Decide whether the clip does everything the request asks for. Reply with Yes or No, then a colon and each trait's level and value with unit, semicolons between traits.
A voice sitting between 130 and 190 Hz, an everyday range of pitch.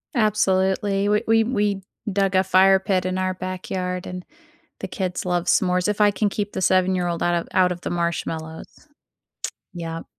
No: medium, 185 Hz; narrow, 1.9 semitones